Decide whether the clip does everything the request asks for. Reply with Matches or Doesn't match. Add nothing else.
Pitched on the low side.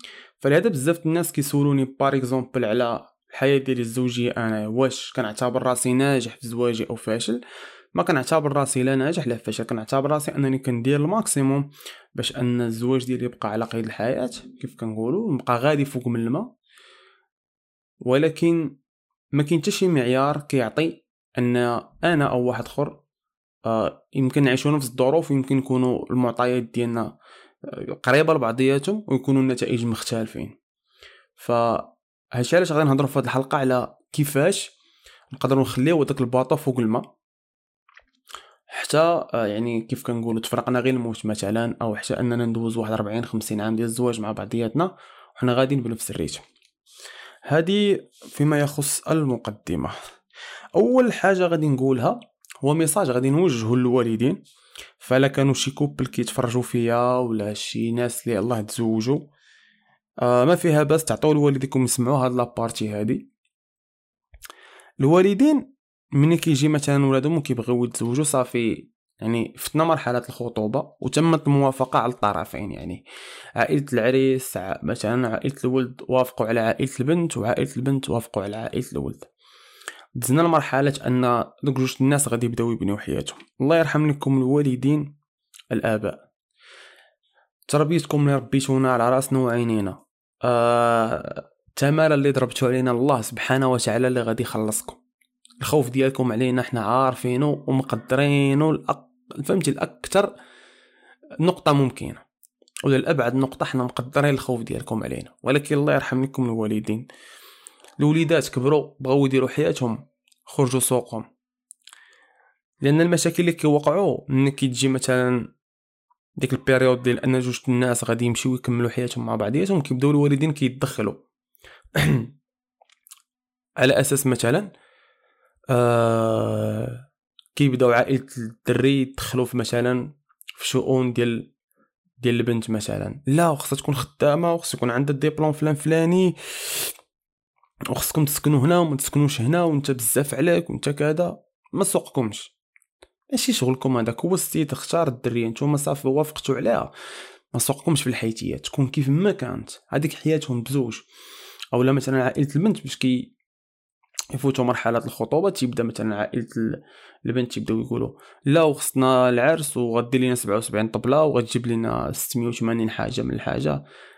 Matches